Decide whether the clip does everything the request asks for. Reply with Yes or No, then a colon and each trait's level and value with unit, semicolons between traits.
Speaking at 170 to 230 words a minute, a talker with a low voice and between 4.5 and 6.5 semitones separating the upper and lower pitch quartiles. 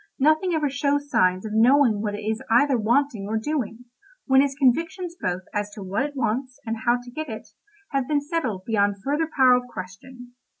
No: average, 200 wpm; very high, 250 Hz; average, 4.8 semitones